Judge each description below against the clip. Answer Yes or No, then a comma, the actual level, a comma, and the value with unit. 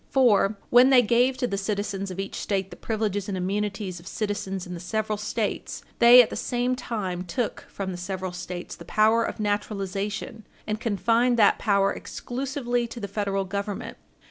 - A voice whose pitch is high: Yes, high, 205 Hz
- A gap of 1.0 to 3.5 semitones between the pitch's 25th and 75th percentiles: Yes, average, 3.1 semitones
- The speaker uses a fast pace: No, average, 180 wpm